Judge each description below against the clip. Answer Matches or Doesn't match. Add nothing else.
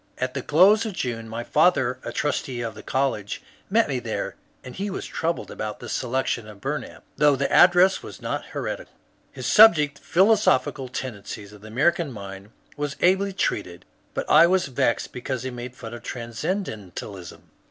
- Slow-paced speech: Doesn't match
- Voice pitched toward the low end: Matches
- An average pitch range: Doesn't match